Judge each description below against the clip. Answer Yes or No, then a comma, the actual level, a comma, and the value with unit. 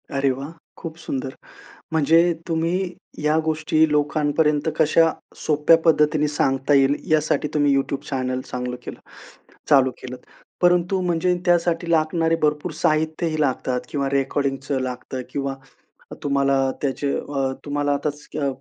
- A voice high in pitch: No, medium, 150 Hz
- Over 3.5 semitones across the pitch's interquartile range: No, average, 2.7 semitones